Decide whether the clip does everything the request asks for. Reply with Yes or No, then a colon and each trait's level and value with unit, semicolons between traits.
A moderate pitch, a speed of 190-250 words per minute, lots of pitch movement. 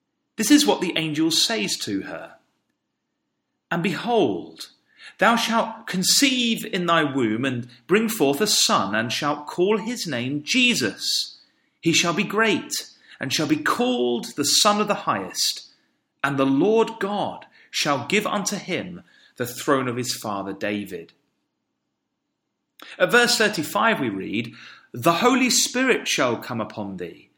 No: medium, 180 Hz; average, 145 wpm; wide, 8.8 semitones